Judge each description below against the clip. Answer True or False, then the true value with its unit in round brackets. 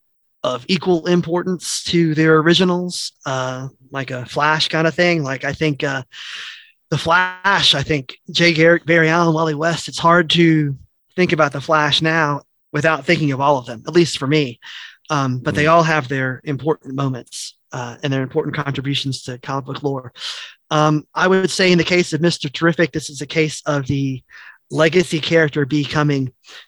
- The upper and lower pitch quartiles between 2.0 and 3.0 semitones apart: False (3.4 semitones)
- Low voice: False (155 Hz)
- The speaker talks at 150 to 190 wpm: True (180 wpm)